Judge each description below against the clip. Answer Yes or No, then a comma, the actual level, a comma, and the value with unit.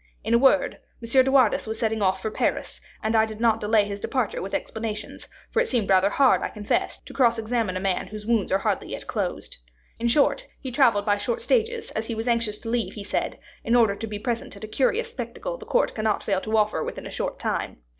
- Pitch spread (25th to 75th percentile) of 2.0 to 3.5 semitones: Yes, average, 3.0 semitones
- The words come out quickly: Yes, fast, 240 wpm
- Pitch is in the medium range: No, high, 225 Hz